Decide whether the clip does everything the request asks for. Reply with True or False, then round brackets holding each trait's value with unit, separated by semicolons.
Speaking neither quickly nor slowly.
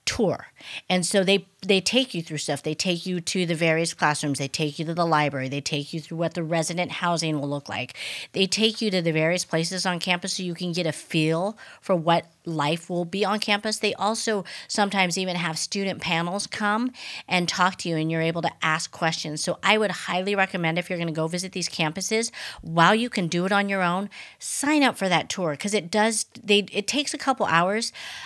False (230 wpm)